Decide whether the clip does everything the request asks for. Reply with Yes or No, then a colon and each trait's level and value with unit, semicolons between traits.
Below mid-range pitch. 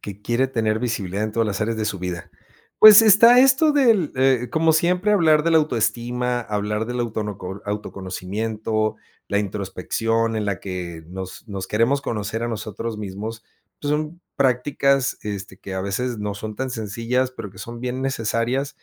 Yes: low, 115 Hz